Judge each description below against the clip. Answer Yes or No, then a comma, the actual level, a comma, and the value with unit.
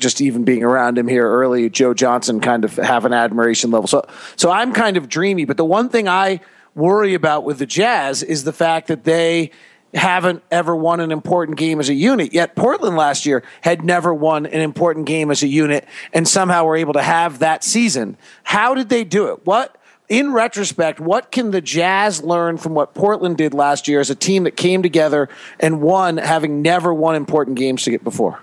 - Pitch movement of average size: Yes, average, 3.9 semitones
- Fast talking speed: Yes, fast, 215 wpm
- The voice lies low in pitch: No, medium, 160 Hz